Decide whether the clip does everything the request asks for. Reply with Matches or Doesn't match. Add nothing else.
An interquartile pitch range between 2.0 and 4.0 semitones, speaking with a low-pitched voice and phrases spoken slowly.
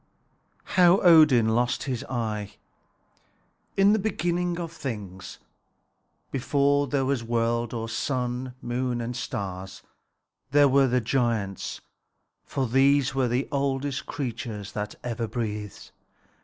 Matches